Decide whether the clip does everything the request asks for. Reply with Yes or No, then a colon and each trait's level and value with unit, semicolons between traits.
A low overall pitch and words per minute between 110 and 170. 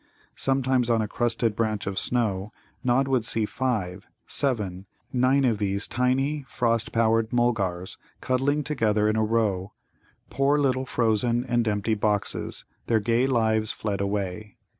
Yes: low, 115 Hz; average, 140 wpm